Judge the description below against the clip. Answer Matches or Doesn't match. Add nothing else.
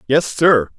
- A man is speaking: Matches